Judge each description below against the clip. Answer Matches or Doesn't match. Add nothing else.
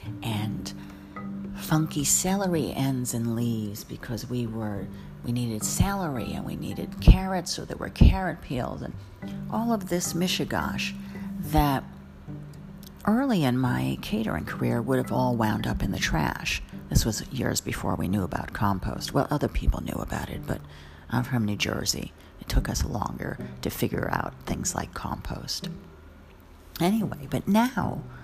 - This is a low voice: Matches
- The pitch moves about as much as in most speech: Doesn't match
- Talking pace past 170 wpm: Doesn't match